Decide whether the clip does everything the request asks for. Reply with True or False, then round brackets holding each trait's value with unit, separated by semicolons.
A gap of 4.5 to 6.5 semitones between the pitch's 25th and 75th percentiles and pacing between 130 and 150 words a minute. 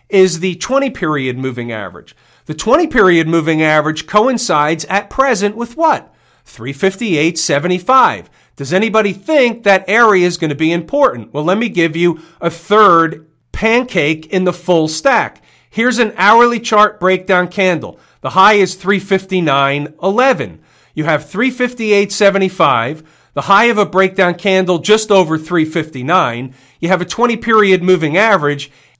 True (5.2 semitones; 140 wpm)